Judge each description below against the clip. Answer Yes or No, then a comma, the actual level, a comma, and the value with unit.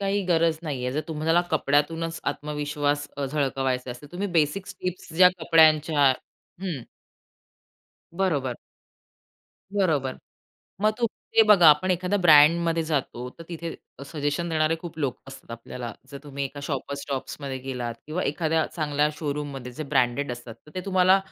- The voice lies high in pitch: No, medium, 150 Hz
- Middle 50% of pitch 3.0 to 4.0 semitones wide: Yes, average, 3.3 semitones